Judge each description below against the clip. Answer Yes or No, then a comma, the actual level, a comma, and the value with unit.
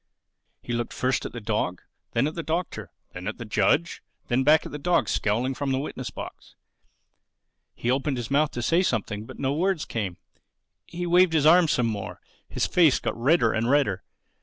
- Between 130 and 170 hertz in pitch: Yes, low, 135 Hz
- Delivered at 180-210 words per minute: Yes, average, 195 wpm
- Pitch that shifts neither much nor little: No, wide, 5.7 semitones